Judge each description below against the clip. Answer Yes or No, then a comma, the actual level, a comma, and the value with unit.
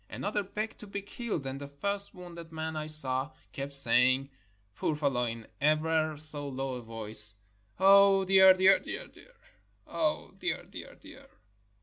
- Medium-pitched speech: Yes, medium, 155 Hz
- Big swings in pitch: Yes, wide, 6.3 semitones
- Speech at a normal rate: Yes, average, 155 wpm